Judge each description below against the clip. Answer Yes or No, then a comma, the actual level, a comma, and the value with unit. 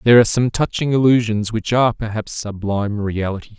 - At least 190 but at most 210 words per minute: No, average, 170 wpm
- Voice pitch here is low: Yes, low, 110 Hz